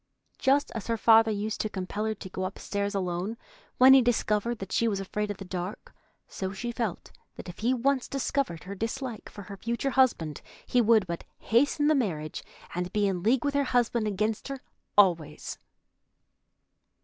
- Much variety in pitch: No, average, 4.3 semitones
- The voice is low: No, high, 215 Hz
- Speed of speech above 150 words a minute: Yes, average, 185 wpm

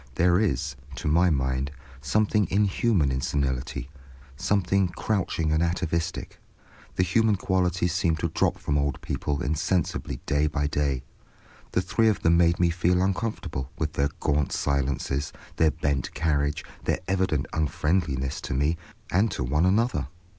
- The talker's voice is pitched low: Yes, very low, 80 Hz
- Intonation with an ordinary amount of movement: Yes, average, 4.4 semitones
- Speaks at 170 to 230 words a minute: No, average, 145 wpm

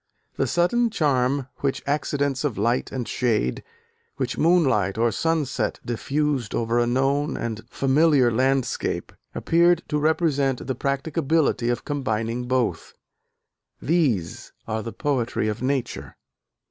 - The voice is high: No, low, 135 Hz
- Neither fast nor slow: No, slow, 120 wpm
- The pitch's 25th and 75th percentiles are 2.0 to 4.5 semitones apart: Yes, average, 3.9 semitones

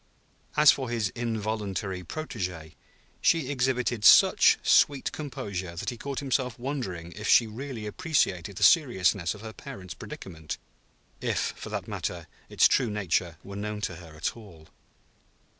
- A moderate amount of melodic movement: No, wide, 5.9 semitones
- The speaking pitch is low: Yes, low, 105 Hz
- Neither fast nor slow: Yes, average, 145 wpm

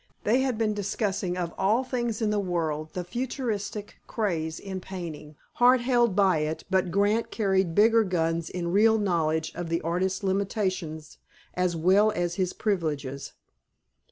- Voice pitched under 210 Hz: Yes, high, 190 Hz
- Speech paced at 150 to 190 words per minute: Yes, average, 155 wpm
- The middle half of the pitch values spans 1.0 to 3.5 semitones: No, average, 4.2 semitones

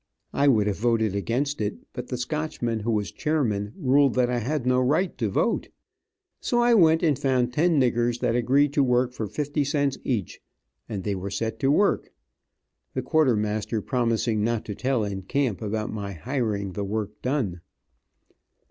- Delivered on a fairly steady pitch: No, average, 4.9 semitones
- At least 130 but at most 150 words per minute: No, average, 175 wpm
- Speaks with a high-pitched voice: No, low, 120 Hz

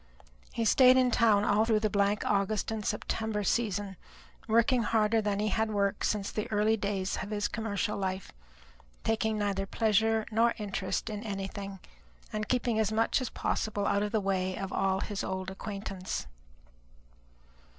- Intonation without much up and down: Yes, narrow, 2.0 semitones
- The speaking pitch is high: Yes, high, 210 Hz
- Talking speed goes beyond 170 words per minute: No, average, 160 wpm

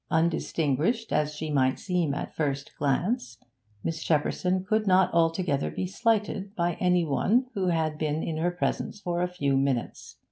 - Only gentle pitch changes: No, average, 3.7 semitones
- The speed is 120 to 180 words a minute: Yes, average, 170 wpm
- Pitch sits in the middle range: Yes, medium, 170 Hz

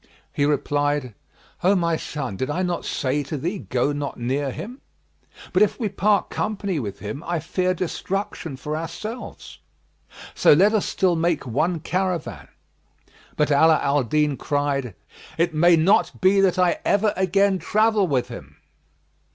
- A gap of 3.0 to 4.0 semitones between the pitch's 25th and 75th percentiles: No, average, 4.8 semitones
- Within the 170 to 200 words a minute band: No, average, 155 wpm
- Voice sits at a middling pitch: Yes, medium, 165 Hz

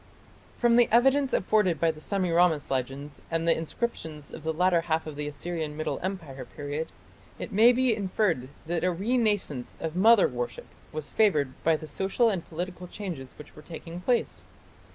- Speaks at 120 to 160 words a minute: No, average, 175 wpm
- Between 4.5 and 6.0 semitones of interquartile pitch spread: Yes, average, 5.0 semitones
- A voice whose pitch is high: No, medium, 170 Hz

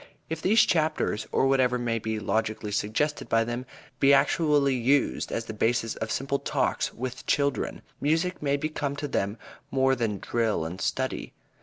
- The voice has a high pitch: No, low, 130 Hz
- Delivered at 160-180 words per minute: Yes, average, 165 wpm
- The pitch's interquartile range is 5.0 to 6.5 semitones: No, average, 4.2 semitones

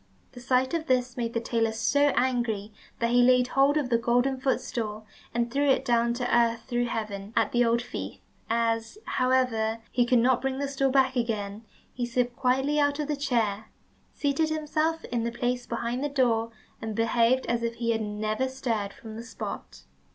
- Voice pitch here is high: Yes, high, 240 Hz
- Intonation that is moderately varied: No, narrow, 2.3 semitones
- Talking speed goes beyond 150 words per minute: Yes, average, 195 wpm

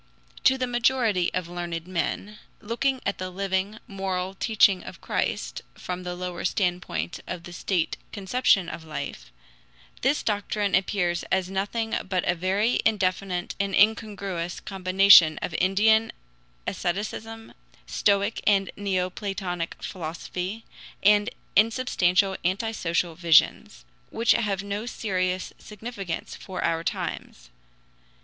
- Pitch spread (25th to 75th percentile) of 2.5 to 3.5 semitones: Yes, average, 2.8 semitones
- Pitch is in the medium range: No, high, 195 Hz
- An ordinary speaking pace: No, slow, 115 wpm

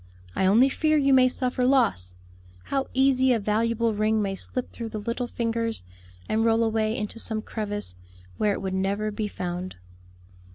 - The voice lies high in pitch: Yes, high, 225 Hz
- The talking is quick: No, average, 170 wpm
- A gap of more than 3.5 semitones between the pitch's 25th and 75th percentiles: No, average, 3.2 semitones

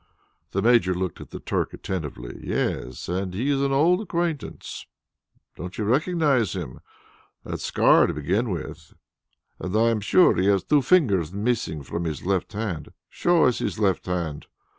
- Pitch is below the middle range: Yes, low, 100 Hz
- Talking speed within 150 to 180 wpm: Yes, average, 170 wpm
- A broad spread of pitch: Yes, wide, 6.8 semitones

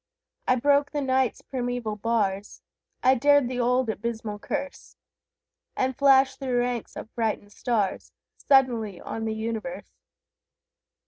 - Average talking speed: No, slow, 125 wpm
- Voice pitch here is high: Yes, high, 245 Hz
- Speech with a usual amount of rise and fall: Yes, average, 3.2 semitones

